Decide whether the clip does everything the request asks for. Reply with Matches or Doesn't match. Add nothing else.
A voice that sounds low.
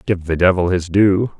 Matches